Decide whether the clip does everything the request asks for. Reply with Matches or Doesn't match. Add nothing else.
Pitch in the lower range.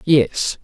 Doesn't match